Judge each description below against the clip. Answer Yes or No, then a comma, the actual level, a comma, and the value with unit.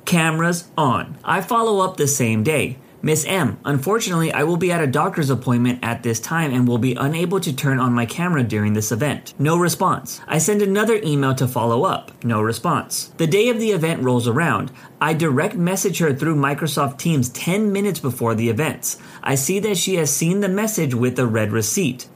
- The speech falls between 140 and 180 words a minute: No, fast, 205 wpm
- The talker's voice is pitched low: No, medium, 150 Hz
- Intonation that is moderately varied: No, wide, 5.9 semitones